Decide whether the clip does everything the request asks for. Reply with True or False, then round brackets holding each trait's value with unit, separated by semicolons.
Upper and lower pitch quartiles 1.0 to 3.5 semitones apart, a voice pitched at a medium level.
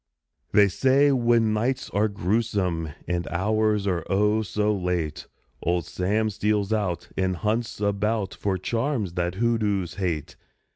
False (3.2 semitones; 105 Hz)